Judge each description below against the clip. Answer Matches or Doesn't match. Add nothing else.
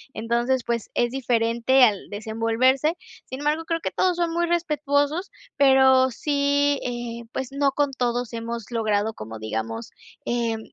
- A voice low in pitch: Doesn't match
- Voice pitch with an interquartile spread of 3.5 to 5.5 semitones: Matches